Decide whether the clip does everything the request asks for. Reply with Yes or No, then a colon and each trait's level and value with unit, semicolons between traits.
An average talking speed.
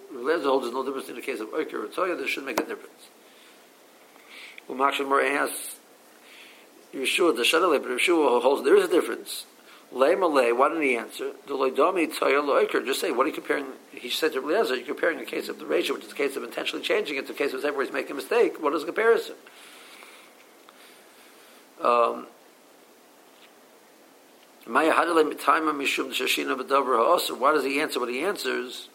Yes: average, 170 wpm